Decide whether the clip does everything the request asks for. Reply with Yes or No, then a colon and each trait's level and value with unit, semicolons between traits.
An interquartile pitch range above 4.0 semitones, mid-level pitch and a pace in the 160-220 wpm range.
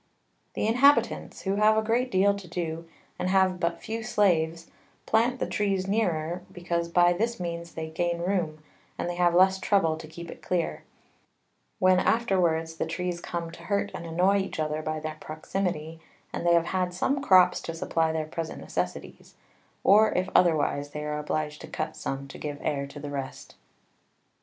No: average, 3.2 semitones; medium, 175 Hz; average, 180 wpm